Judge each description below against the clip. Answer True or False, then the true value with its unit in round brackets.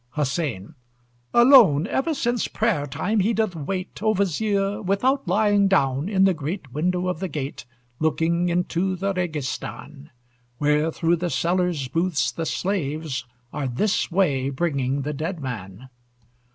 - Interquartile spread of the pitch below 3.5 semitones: False (5.2 semitones)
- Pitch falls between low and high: True (170 Hz)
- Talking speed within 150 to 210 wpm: False (140 wpm)